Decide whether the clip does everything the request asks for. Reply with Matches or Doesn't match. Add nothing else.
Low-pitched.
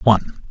Matches